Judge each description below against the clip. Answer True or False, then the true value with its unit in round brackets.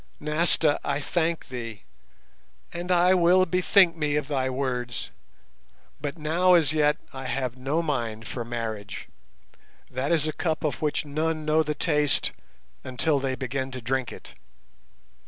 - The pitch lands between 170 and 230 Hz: False (145 Hz)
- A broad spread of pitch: False (3.8 semitones)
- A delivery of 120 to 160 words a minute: True (150 wpm)